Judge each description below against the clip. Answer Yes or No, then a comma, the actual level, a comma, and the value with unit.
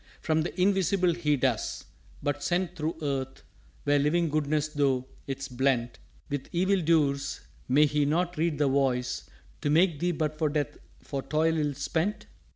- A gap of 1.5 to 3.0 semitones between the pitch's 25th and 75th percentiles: No, average, 3.4 semitones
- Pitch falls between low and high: Yes, medium, 150 Hz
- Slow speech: No, average, 165 wpm